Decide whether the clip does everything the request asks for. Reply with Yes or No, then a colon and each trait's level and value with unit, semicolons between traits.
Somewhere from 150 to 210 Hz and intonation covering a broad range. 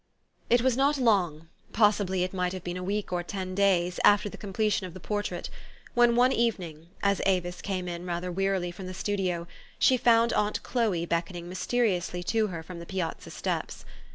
No: high, 190 Hz; average, 3.0 semitones